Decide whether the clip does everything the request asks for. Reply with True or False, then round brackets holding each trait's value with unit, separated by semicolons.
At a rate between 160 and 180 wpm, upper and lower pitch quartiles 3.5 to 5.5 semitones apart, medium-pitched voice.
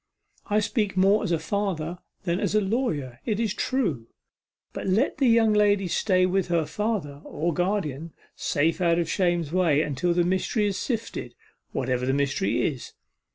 True (170 wpm; 4.8 semitones; 180 Hz)